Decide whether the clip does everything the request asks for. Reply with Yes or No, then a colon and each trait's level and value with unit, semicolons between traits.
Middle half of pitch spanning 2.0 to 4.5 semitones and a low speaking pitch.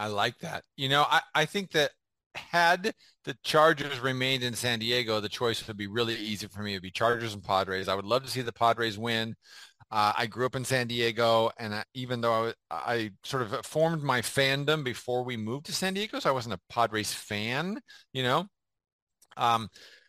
Yes: average, 3.8 semitones; low, 120 Hz